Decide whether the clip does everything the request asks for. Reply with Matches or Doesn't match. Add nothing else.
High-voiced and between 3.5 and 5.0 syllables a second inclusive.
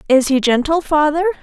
Doesn't match